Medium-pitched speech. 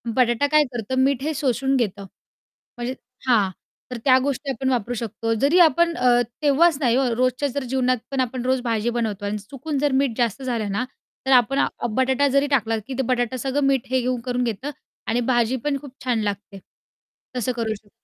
No: very high, 255 Hz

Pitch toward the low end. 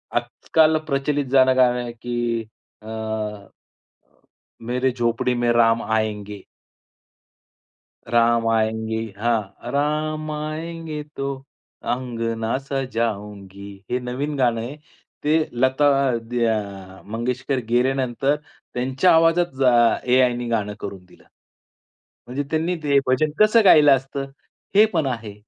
Yes: low, 125 Hz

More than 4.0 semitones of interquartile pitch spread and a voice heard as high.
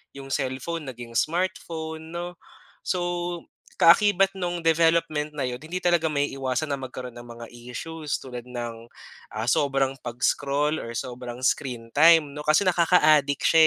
No: average, 4.8 semitones; medium, 150 Hz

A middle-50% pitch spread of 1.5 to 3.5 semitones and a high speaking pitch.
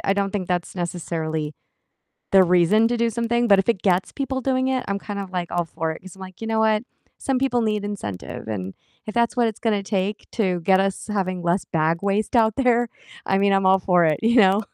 No: average, 4.1 semitones; high, 195 Hz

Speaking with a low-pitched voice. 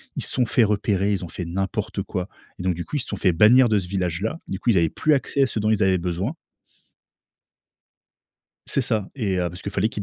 Yes: low, 100 Hz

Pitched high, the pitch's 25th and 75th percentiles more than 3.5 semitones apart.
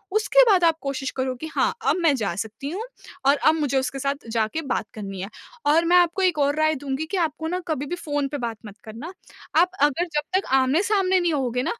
Yes: very high, 290 Hz; average, 4.5 semitones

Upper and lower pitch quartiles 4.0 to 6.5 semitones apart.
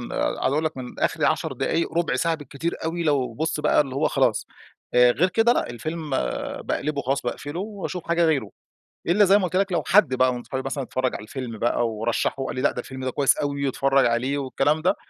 Yes: average, 4.4 semitones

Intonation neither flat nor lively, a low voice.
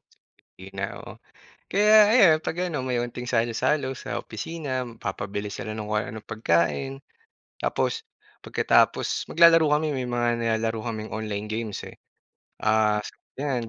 Yes: average, 4.2 semitones; low, 115 Hz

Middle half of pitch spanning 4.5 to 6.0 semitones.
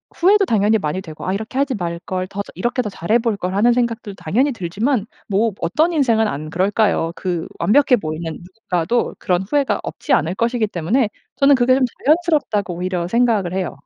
Yes: average, 5.3 semitones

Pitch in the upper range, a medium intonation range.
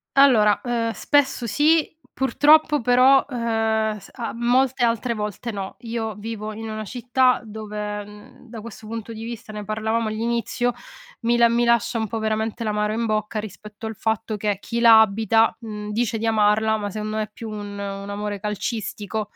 No: high, 220 Hz; narrow, 2.0 semitones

